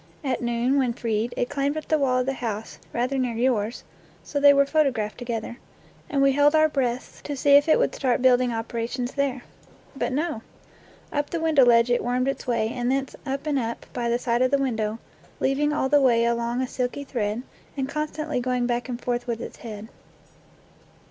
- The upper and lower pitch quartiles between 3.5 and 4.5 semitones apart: No, average, 2.8 semitones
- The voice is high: Yes, very high, 255 Hz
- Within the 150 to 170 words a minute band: No, fast, 205 wpm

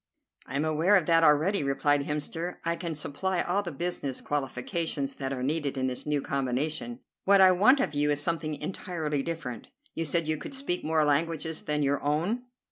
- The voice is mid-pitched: Yes, medium, 155 Hz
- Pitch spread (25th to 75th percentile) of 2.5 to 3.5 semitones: Yes, average, 3.1 semitones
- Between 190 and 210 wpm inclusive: Yes, average, 195 wpm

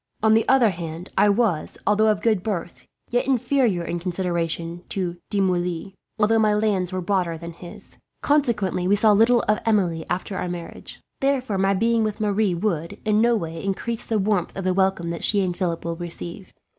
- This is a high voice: Yes, high, 195 Hz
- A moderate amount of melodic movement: Yes, average, 3.9 semitones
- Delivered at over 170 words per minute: Yes, average, 195 wpm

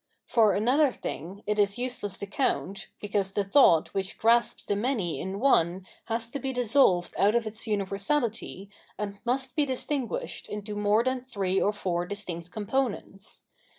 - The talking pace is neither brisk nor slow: Yes, average, 165 wpm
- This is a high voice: Yes, high, 210 Hz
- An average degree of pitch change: Yes, average, 3.9 semitones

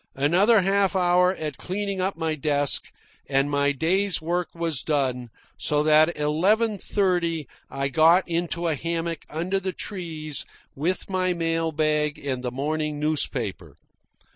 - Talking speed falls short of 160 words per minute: Yes, average, 145 wpm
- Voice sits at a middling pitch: Yes, medium, 165 Hz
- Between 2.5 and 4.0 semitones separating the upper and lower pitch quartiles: Yes, average, 3.4 semitones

